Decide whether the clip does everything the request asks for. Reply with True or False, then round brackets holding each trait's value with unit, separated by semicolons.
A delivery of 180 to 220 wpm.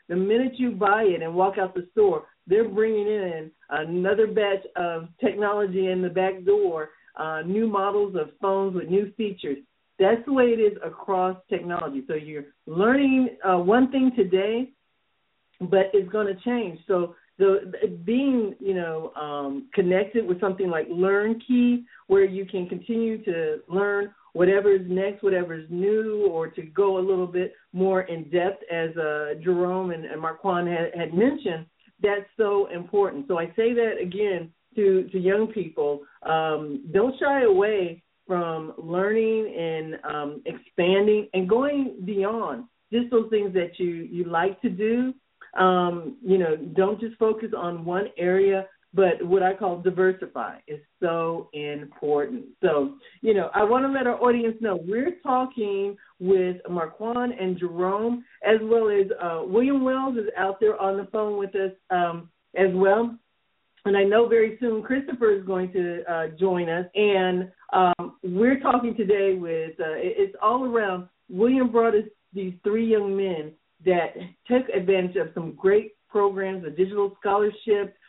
False (160 wpm)